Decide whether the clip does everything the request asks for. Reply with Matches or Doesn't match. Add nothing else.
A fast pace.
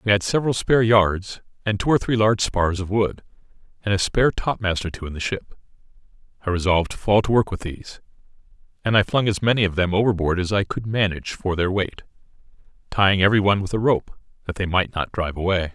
Matches